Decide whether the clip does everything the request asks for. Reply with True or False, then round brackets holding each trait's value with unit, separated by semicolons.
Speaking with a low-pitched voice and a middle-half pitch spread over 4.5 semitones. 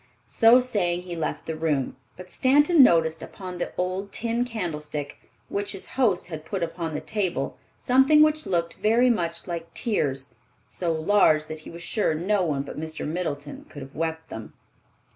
False (175 Hz; 5.1 semitones)